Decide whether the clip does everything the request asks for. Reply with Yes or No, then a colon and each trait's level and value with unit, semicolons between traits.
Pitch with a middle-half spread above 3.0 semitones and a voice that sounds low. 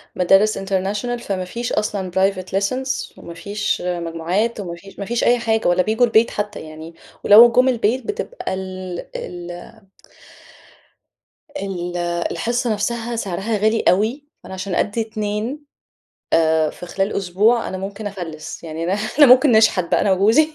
No: average, 3.9 semitones; high, 200 Hz